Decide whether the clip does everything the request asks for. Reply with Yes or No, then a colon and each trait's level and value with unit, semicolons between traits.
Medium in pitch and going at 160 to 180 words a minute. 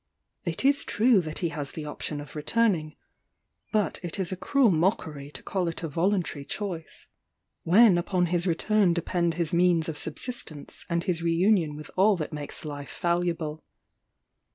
Yes: medium, 170 Hz; average, 170 wpm